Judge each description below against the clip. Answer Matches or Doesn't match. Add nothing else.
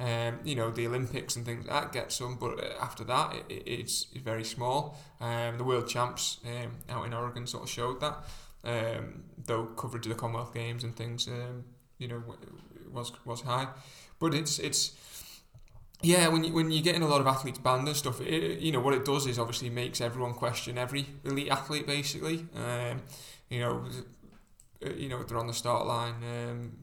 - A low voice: Matches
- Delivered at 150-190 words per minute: Doesn't match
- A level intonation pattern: Doesn't match